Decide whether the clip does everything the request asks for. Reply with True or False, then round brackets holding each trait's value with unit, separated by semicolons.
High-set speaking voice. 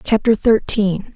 True (205 Hz)